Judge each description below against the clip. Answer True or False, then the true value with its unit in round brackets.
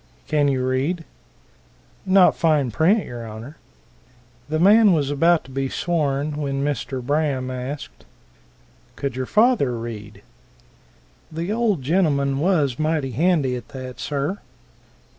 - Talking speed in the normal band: False (125 wpm)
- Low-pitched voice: False (145 Hz)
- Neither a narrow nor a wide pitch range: True (4.3 semitones)